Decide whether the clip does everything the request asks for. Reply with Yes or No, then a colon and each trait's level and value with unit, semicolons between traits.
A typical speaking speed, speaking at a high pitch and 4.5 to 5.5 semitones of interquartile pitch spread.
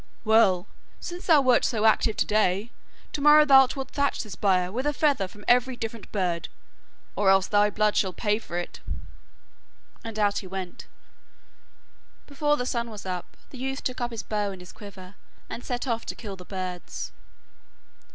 Yes: average, 180 wpm; high, 215 Hz; average, 4.8 semitones